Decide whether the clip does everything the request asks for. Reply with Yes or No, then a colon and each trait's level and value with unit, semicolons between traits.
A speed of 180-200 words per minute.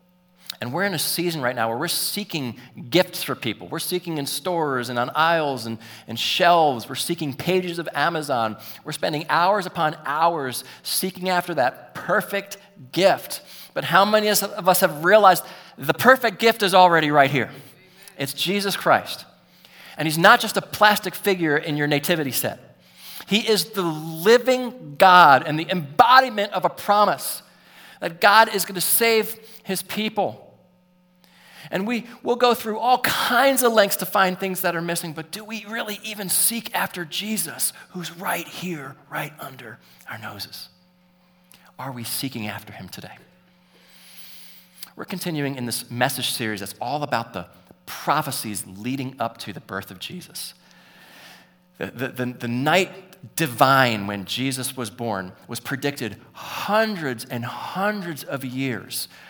No: average, 160 wpm